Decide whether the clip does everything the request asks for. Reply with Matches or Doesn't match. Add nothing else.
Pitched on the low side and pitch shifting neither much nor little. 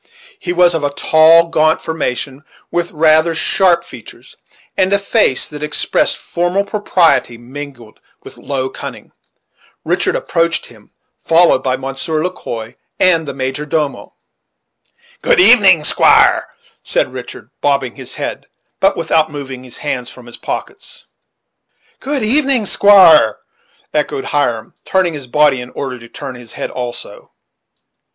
Doesn't match